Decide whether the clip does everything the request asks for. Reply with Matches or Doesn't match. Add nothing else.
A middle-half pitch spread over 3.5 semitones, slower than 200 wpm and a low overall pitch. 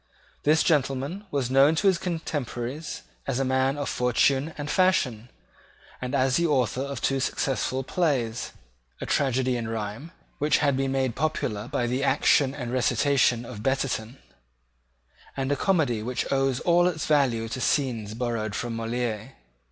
Doesn't match